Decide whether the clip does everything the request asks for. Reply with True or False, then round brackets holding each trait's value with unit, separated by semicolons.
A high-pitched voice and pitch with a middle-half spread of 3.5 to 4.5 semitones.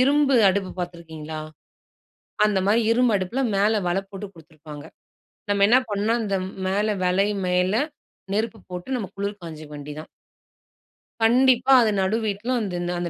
True (200 Hz; 4.2 semitones)